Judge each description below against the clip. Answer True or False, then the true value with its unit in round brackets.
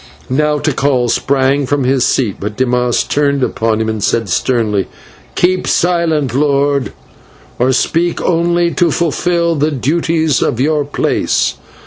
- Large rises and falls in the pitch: False (4.5 semitones)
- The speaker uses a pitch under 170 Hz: True (140 Hz)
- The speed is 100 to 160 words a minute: True (135 wpm)